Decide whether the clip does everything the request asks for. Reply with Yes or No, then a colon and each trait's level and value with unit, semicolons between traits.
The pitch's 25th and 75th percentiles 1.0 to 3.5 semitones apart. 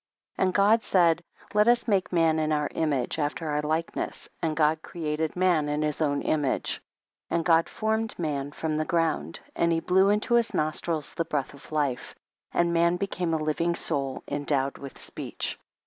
Yes: average, 2.7 semitones